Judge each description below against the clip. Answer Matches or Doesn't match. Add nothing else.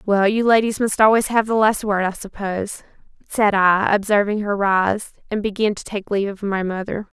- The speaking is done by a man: Doesn't match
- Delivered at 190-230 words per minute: Matches